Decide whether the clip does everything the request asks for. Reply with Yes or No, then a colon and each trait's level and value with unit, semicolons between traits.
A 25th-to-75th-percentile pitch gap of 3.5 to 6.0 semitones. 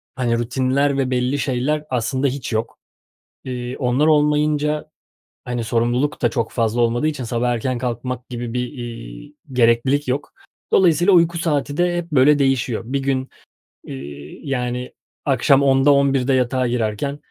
No: average, 3.0 semitones